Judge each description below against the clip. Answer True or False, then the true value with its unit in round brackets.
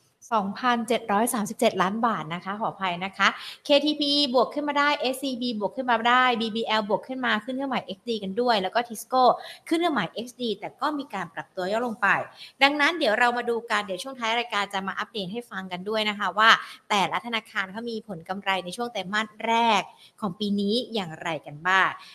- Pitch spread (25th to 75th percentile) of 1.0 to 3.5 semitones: False (4.0 semitones)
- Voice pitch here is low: False (225 Hz)